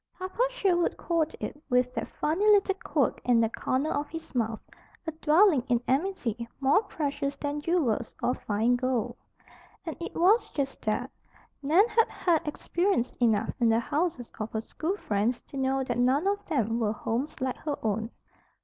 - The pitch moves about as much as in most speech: No, wide, 6.2 semitones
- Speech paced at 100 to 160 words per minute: No, average, 175 wpm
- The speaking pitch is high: Yes, very high, 280 Hz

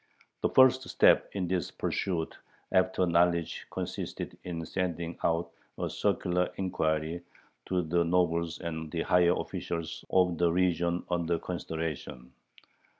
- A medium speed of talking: No, slow, 125 wpm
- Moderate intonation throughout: No, narrow, 1.6 semitones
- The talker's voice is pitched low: Yes, very low, 85 Hz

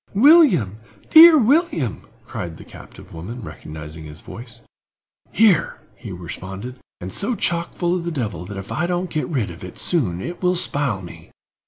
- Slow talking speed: No, average, 165 wpm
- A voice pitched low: Yes, low, 125 Hz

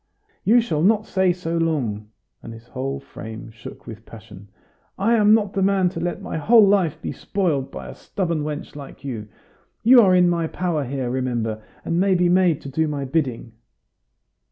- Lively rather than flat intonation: Yes, wide, 6.7 semitones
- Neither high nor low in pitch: Yes, medium, 160 Hz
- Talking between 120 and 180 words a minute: No, average, 190 wpm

